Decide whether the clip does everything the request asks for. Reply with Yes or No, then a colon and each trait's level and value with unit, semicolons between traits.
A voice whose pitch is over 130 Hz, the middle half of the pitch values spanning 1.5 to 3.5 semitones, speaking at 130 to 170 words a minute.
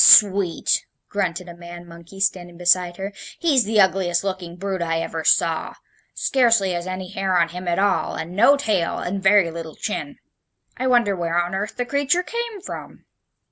No: high, 190 Hz; average, 3.2 semitones; average, 180 wpm